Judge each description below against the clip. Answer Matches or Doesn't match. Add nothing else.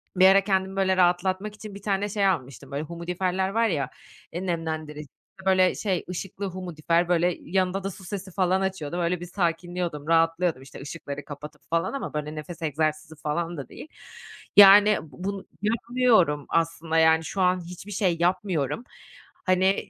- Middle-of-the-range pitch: Matches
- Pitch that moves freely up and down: Doesn't match